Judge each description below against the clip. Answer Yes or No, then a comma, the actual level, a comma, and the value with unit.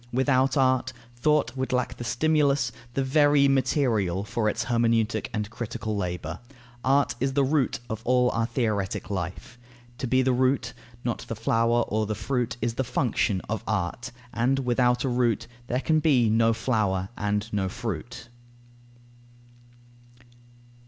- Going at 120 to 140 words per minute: No, average, 150 wpm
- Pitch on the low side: Yes, low, 120 Hz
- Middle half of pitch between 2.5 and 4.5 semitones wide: Yes, average, 3.2 semitones